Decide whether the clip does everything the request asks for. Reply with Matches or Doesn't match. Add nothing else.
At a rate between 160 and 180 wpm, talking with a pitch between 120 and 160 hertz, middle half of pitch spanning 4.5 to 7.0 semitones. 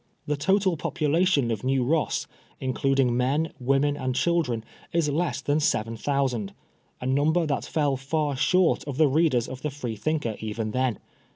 Doesn't match